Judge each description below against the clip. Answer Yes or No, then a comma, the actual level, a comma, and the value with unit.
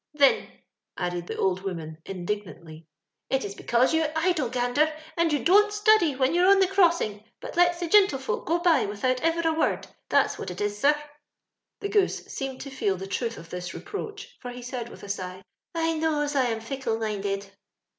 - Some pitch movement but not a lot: No, wide, 8.7 semitones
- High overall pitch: Yes, very high, 265 Hz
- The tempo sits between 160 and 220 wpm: Yes, average, 195 wpm